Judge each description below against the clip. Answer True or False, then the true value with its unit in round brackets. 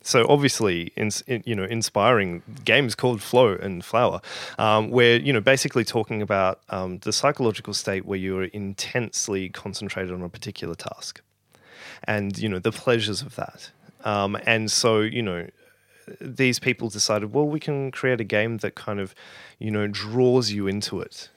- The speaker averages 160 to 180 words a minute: True (175 wpm)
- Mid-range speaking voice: False (110 Hz)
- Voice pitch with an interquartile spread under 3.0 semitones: False (3.9 semitones)